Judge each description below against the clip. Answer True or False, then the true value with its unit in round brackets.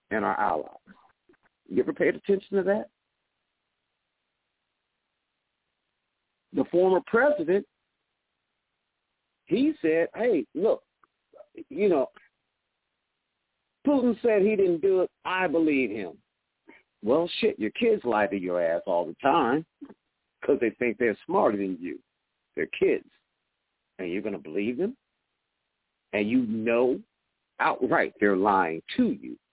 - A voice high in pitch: True (200 Hz)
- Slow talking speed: True (125 wpm)